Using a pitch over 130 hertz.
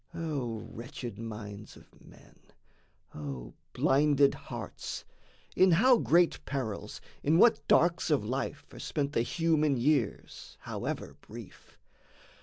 Yes: medium, 140 Hz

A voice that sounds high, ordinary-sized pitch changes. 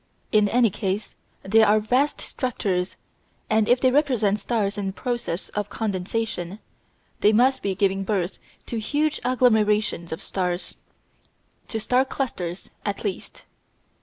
Yes: high, 215 Hz; average, 4.0 semitones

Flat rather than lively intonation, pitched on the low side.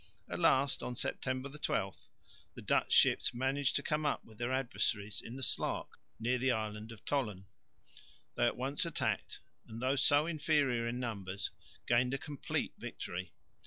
No: average, 3.7 semitones; low, 125 Hz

